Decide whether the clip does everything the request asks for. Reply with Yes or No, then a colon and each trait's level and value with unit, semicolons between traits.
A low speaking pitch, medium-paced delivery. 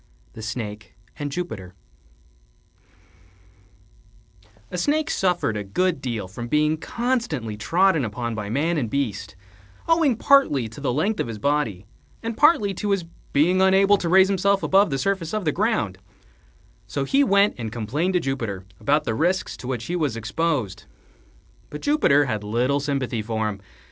No: medium, 145 Hz; average, 160 wpm